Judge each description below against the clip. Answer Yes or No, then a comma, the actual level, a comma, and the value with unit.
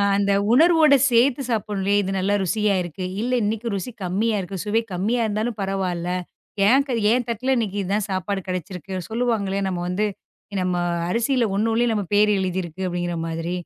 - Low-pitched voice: No, high, 205 Hz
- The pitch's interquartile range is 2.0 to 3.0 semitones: No, average, 3.7 semitones